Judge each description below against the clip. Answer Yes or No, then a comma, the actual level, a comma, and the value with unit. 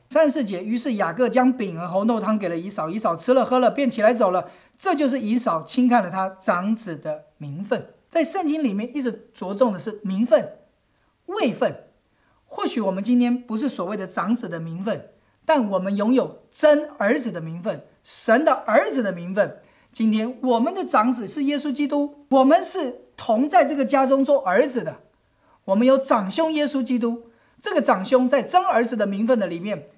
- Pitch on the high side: Yes, high, 240 Hz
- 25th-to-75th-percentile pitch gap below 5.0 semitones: No, wide, 5.5 semitones